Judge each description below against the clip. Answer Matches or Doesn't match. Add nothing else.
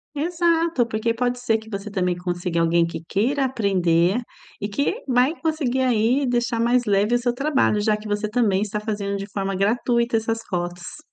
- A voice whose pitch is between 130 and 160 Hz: Doesn't match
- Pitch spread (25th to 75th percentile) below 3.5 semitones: Doesn't match